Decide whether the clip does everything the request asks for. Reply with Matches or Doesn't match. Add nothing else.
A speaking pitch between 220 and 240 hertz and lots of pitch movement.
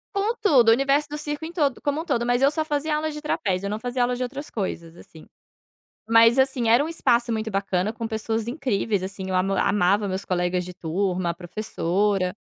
Matches